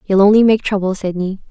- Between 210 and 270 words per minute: No, average, 200 wpm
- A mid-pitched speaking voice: No, high, 200 Hz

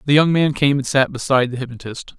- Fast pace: Yes, fast, 245 wpm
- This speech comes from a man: Yes, male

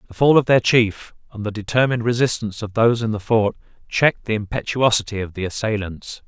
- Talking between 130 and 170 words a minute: No, average, 190 wpm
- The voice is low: Yes, low, 110 Hz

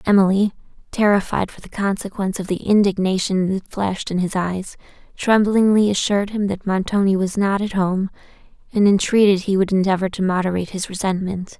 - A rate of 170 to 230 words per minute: No, average, 160 wpm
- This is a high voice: Yes, high, 195 Hz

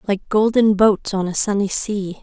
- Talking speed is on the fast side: No, average, 190 wpm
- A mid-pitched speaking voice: No, high, 205 Hz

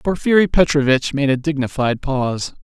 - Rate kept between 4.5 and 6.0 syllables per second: Yes, 5.3 syllables/s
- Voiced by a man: Yes, male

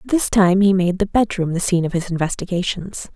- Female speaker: Yes, female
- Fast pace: Yes, fast, 210 wpm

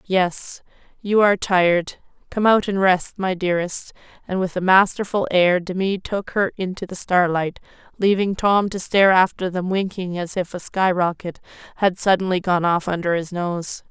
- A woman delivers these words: Yes, female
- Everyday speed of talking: Yes, average, 175 wpm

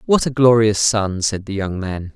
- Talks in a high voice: No, low, 105 Hz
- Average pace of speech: No, fast, 225 wpm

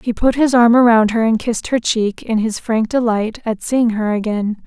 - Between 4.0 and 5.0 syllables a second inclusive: Yes, 4.8 syllables/s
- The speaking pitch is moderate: No, high, 225 Hz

